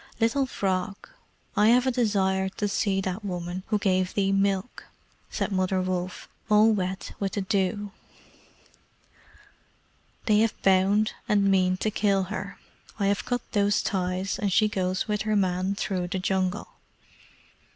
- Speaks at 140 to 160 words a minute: Yes, average, 150 wpm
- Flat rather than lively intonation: Yes, narrow, 2.1 semitones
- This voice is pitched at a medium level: No, high, 195 Hz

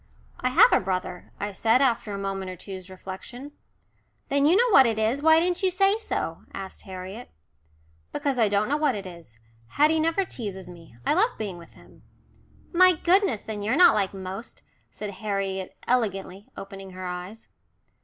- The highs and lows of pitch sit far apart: Yes, wide, 7.4 semitones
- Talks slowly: No, average, 180 wpm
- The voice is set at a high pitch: Yes, high, 210 Hz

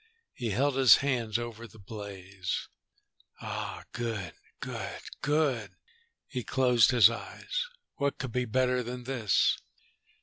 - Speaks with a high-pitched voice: No, low, 120 Hz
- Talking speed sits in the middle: No, slow, 125 wpm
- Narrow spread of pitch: No, average, 3.2 semitones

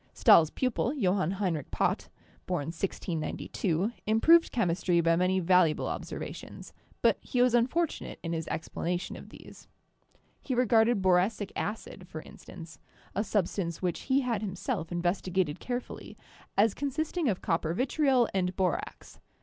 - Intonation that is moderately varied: No, wide, 5.7 semitones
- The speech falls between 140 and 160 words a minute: Yes, average, 150 wpm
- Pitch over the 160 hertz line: Yes, high, 190 Hz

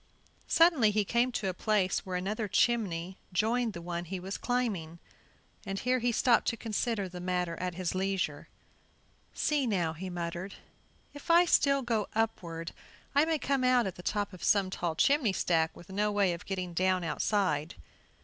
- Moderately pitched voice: No, high, 195 Hz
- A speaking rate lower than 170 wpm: No, average, 180 wpm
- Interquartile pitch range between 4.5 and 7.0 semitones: Yes, average, 4.9 semitones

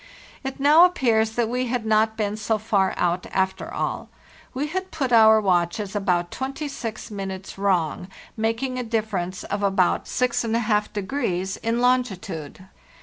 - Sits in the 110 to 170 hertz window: No, high, 220 Hz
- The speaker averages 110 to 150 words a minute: Yes, average, 140 wpm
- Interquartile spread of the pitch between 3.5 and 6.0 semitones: Yes, average, 4.4 semitones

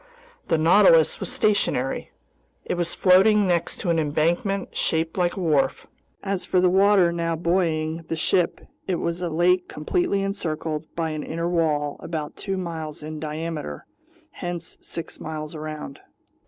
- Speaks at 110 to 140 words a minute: No, average, 155 wpm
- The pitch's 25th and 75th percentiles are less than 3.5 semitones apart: Yes, average, 2.7 semitones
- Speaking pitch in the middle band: Yes, medium, 165 Hz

